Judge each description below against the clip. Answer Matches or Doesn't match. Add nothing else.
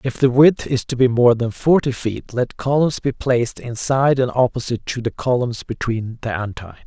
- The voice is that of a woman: Doesn't match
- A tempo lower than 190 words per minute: Doesn't match